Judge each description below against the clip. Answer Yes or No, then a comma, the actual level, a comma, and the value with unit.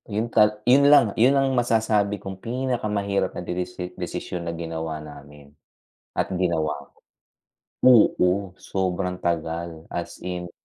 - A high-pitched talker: No, very low, 90 Hz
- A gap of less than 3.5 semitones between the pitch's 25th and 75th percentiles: No, average, 4.3 semitones